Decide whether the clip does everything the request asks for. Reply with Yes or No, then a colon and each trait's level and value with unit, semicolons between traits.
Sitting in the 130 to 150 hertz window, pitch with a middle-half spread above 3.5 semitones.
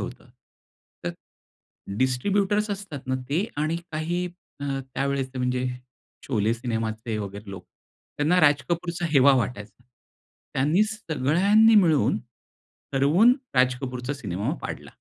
Yes: medium, 140 Hz; wide, 5.6 semitones